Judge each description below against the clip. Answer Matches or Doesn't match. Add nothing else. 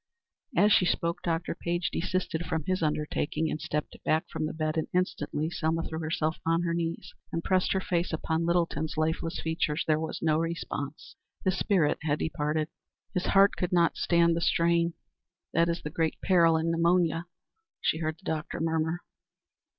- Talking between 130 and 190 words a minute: Matches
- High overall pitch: Doesn't match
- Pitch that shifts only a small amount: Matches